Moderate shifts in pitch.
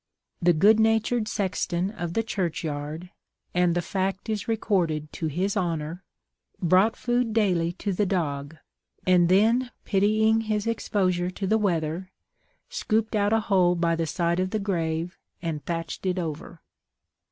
Yes: average, 4.0 semitones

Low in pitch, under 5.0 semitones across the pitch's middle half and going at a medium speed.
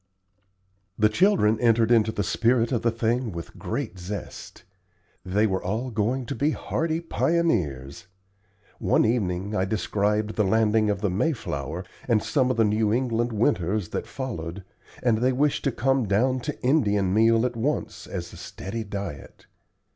Yes: low, 110 Hz; average, 3.6 semitones; average, 160 wpm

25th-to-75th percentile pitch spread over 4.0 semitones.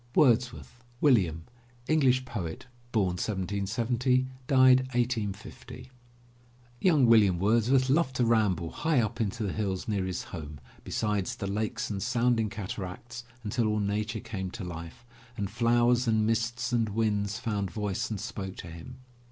No: average, 3.7 semitones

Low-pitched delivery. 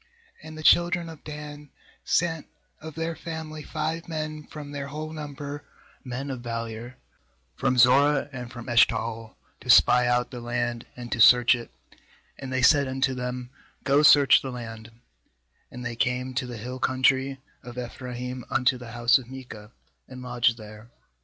Yes: low, 130 Hz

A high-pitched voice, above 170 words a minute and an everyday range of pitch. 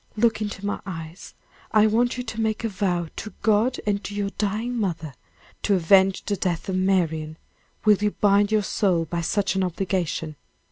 Yes: high, 200 Hz; average, 185 wpm; average, 3.2 semitones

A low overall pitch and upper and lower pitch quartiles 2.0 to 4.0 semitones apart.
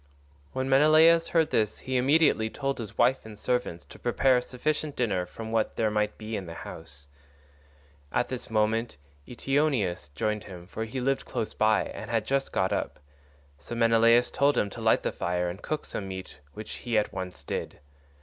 No: low, 115 Hz; average, 4.5 semitones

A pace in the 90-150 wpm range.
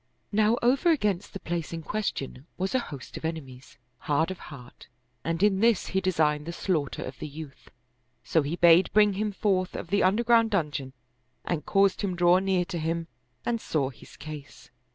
No: average, 185 wpm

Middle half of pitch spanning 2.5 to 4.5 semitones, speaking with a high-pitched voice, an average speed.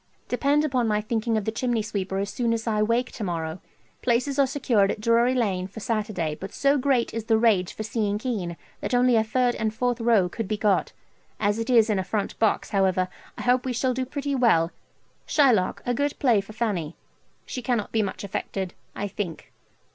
No: average, 3.6 semitones; high, 225 Hz; fast, 210 wpm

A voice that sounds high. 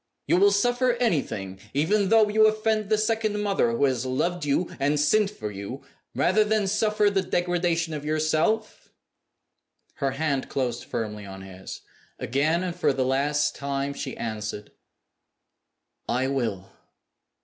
No: medium, 155 Hz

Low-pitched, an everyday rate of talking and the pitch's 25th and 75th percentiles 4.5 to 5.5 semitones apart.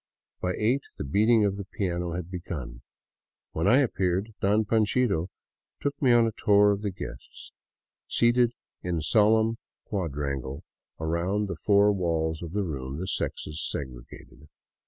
Yes: very low, 95 Hz; average, 155 wpm; average, 5.0 semitones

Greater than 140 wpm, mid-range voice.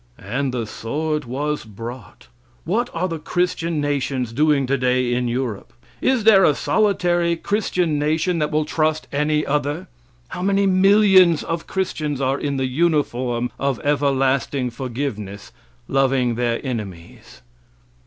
No: slow, 135 wpm; medium, 145 Hz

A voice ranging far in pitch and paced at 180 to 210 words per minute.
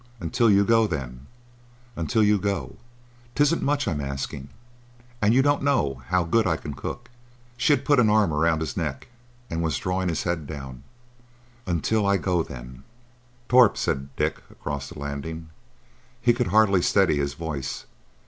No: wide, 7.3 semitones; average, 155 wpm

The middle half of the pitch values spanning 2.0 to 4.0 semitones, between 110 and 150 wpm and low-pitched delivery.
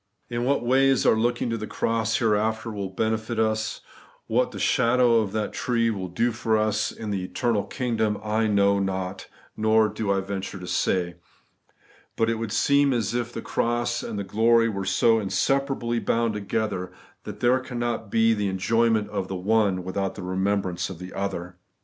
No: average, 2.9 semitones; average, 185 wpm; low, 110 Hz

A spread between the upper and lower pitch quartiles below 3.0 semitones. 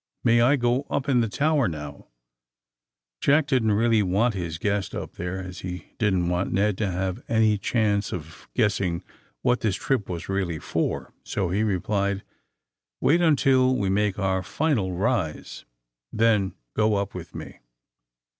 No: average, 4.4 semitones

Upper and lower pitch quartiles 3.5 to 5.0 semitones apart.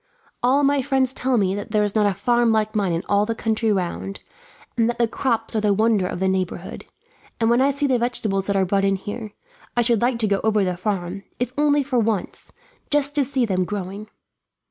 Yes: average, 3.8 semitones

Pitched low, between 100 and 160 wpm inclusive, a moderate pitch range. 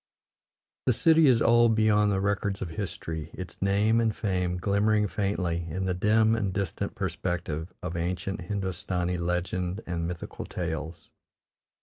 Yes: very low, 95 Hz; average, 140 wpm; average, 3.2 semitones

